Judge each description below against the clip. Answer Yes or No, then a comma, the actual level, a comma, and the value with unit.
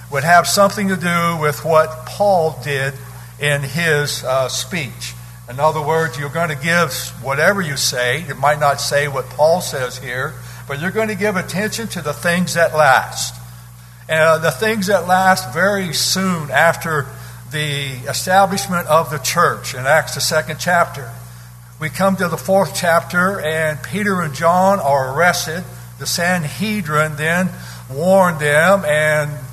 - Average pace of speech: Yes, average, 160 wpm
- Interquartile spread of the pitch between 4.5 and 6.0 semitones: Yes, average, 4.9 semitones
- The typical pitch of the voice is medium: Yes, medium, 155 Hz